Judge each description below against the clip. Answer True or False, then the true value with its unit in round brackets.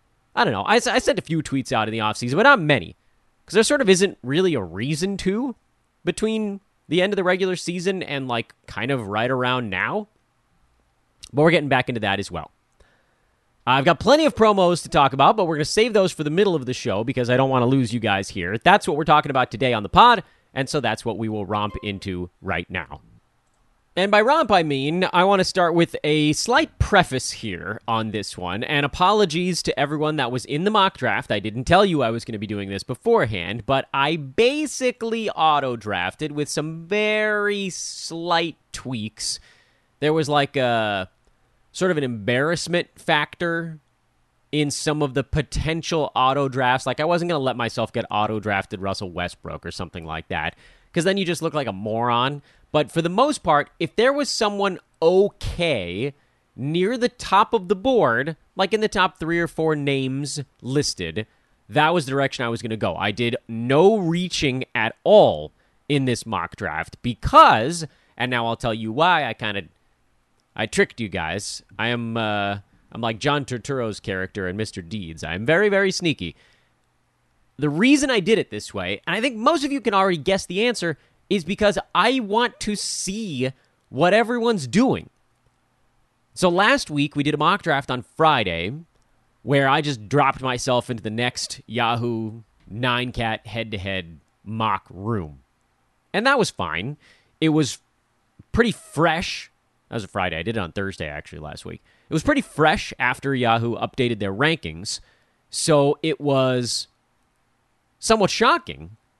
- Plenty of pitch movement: True (7.6 semitones)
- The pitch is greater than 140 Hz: False (135 Hz)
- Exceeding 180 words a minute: True (190 wpm)